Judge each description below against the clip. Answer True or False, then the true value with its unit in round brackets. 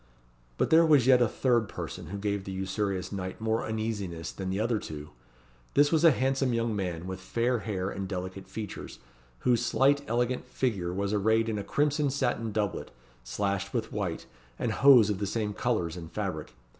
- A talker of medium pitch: False (105 Hz)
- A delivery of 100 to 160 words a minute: False (185 wpm)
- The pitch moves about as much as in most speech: True (4.2 semitones)